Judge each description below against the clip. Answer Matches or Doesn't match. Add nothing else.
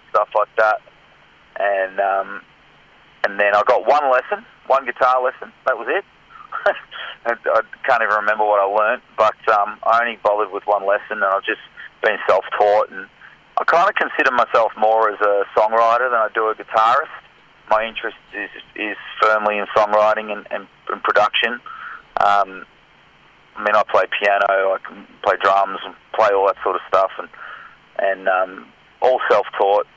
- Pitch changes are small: Matches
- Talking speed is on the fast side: Doesn't match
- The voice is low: Matches